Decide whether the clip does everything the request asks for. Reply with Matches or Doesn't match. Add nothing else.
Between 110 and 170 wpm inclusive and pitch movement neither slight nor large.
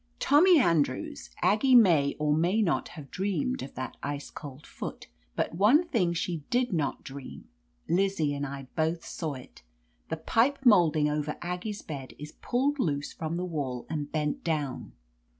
Doesn't match